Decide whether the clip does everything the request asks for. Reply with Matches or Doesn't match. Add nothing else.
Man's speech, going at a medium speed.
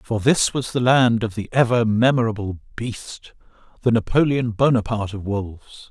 Matches